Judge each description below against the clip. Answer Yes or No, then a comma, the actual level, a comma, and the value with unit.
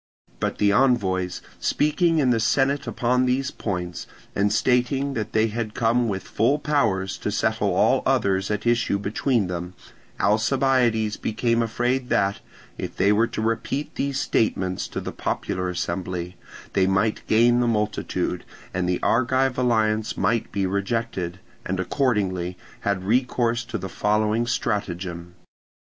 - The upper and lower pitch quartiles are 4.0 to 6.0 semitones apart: Yes, average, 4.3 semitones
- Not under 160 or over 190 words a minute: No, average, 145 wpm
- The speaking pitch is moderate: No, low, 110 Hz